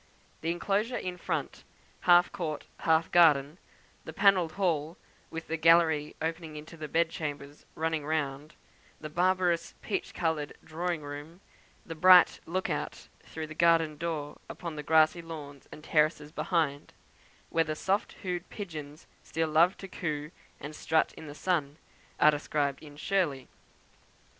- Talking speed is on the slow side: No, average, 150 wpm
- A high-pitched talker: No, medium, 160 Hz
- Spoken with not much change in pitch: Yes, narrow, 2.3 semitones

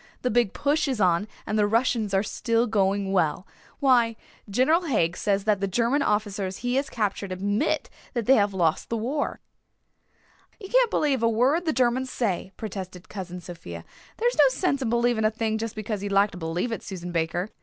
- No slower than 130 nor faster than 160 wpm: No, average, 200 wpm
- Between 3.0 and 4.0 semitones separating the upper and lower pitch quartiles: No, average, 4.4 semitones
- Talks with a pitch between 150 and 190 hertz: No, high, 215 Hz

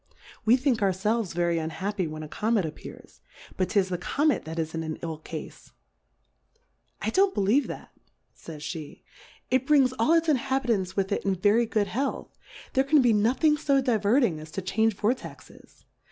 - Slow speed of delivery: No, average, 180 wpm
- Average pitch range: No, wide, 6.5 semitones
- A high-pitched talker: Yes, high, 210 Hz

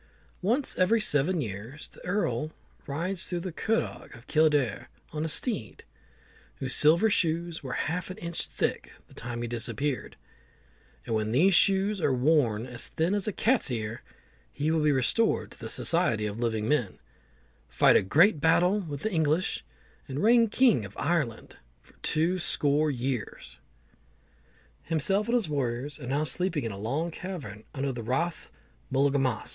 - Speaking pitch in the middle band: Yes, medium, 150 Hz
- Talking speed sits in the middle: Yes, average, 165 wpm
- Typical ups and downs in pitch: No, wide, 6.5 semitones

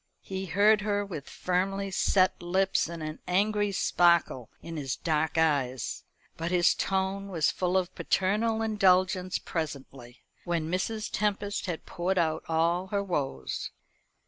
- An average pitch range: Yes, average, 3.4 semitones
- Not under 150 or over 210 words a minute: No, average, 140 wpm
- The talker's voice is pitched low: No, medium, 180 Hz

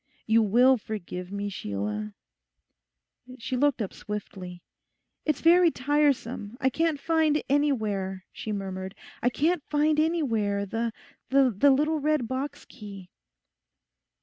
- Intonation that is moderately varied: No, wide, 6.5 semitones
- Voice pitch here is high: Yes, high, 240 Hz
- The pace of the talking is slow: Yes, slow, 115 wpm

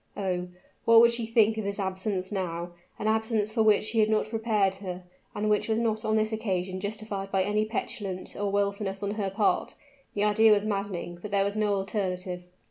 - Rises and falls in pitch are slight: Yes, narrow, 2.1 semitones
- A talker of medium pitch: No, high, 205 Hz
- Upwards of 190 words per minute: Yes, fast, 205 wpm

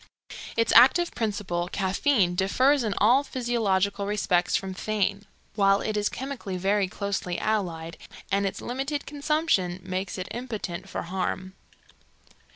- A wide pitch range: No, average, 4.3 semitones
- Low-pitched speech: No, high, 200 Hz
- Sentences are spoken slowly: Yes, slow, 130 wpm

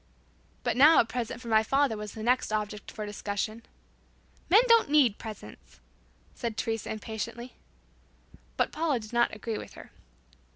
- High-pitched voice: Yes, high, 225 Hz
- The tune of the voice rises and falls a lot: No, average, 2.9 semitones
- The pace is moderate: Yes, average, 155 wpm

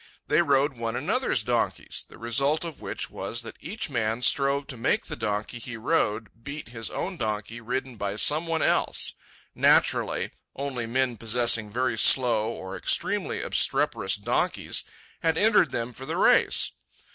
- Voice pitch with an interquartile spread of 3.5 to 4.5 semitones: Yes, average, 3.9 semitones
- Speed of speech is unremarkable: Yes, average, 155 wpm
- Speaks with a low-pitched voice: Yes, low, 120 Hz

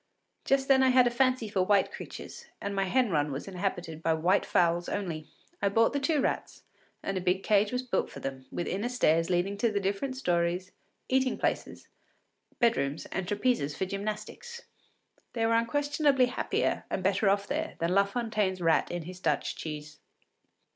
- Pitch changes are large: Yes, wide, 6.0 semitones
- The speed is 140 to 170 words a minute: No, average, 180 wpm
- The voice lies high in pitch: Yes, high, 200 Hz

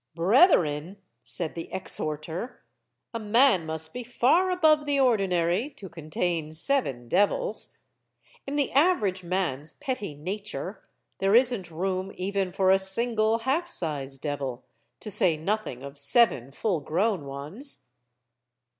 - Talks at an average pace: No, slow, 130 wpm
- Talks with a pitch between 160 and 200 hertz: Yes, high, 190 Hz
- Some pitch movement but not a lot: No, wide, 7.1 semitones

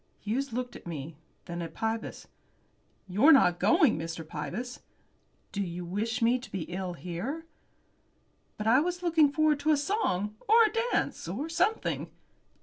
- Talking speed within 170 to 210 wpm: No, average, 155 wpm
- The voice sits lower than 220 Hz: No, high, 230 Hz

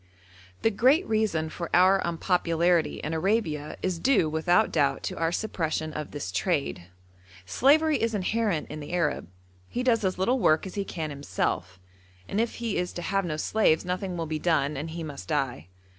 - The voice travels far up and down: No, average, 4.7 semitones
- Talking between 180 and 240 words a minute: Yes, average, 185 wpm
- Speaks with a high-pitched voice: No, medium, 170 Hz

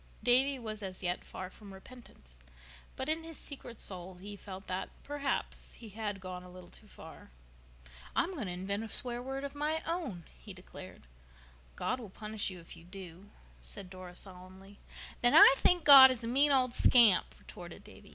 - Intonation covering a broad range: Yes, wide, 6.0 semitones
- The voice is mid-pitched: No, high, 210 Hz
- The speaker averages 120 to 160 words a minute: No, average, 185 wpm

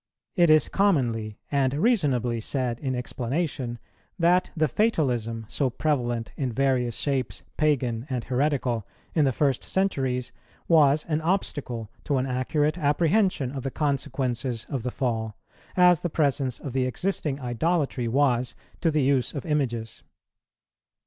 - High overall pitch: No, low, 135 Hz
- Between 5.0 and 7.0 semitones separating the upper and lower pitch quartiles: No, average, 3.9 semitones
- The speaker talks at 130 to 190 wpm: Yes, average, 140 wpm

